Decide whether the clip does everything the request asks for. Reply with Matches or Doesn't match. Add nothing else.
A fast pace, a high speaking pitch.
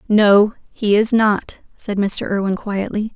Doesn't match